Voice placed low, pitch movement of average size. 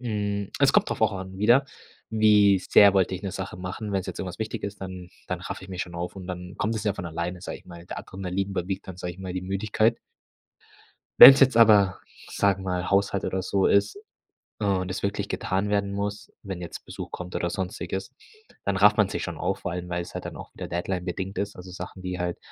No: very low, 95 Hz; narrow, 2.0 semitones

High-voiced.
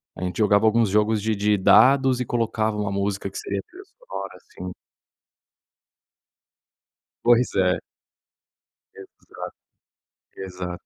No: low, 105 Hz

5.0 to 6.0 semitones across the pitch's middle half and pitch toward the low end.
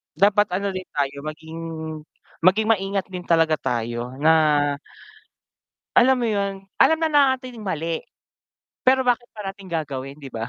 No: wide, 5.5 semitones; medium, 185 Hz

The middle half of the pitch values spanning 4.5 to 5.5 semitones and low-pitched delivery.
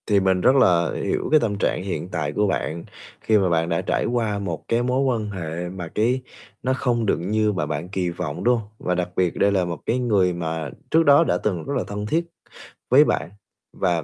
Yes: average, 4.9 semitones; very low, 95 Hz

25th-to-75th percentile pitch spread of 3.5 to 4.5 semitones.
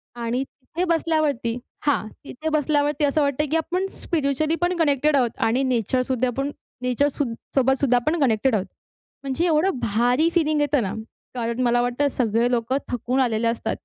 Yes: average, 3.8 semitones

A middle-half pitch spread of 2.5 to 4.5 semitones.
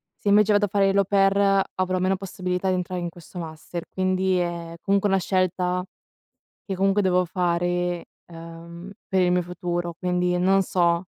No: narrow, 1.7 semitones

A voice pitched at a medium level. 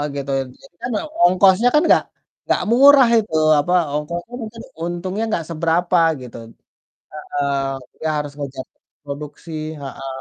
Yes: medium, 170 Hz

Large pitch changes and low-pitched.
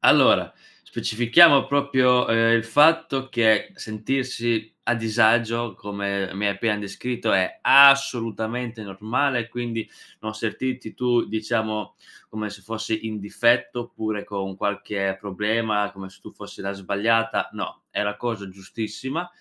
No: average, 2.8 semitones; low, 110 Hz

